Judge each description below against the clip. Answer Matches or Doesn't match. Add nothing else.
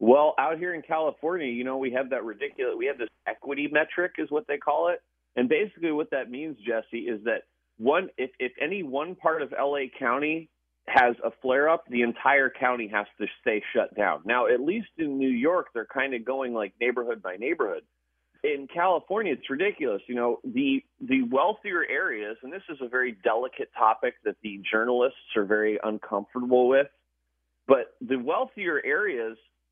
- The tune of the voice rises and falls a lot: Matches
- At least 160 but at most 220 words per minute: Matches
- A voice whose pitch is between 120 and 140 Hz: Matches